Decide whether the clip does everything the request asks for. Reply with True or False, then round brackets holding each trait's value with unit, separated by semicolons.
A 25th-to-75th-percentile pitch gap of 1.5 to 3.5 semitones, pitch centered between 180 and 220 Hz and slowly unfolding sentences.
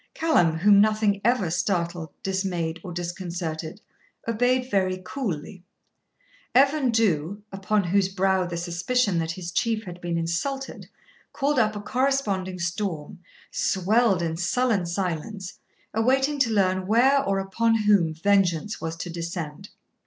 False (4.5 semitones; 190 Hz; 130 wpm)